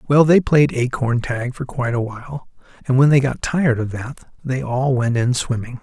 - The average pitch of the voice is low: Yes, low, 130 Hz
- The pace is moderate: No, fast, 215 wpm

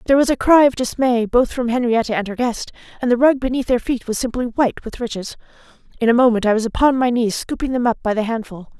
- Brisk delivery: Yes, fast, 250 wpm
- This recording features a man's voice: No, female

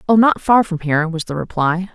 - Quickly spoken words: Yes, fast, 245 wpm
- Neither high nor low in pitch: Yes, medium, 180 Hz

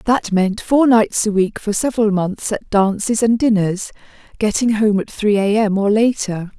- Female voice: Yes, female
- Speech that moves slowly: No, average, 190 wpm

